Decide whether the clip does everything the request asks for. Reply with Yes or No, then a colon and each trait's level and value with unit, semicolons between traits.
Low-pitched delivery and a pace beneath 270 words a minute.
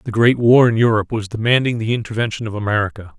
Yes: low, 110 Hz; fast, 205 wpm